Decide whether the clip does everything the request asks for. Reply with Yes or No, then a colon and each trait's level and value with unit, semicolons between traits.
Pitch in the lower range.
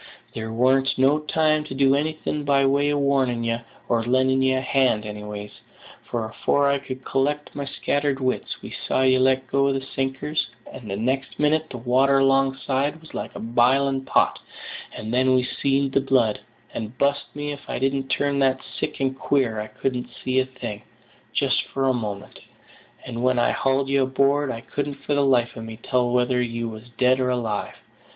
Yes: low, 130 Hz